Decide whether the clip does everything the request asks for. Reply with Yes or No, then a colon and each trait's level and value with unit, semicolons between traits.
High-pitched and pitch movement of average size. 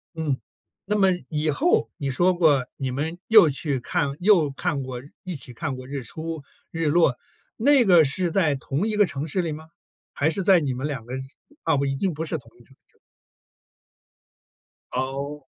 No: medium, 150 Hz; average, 4.4 semitones